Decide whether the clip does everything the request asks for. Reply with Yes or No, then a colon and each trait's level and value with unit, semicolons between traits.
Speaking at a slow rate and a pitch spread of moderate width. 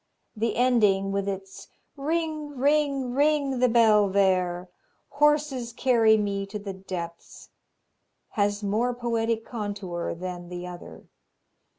Yes: slow, 115 wpm; average, 4.7 semitones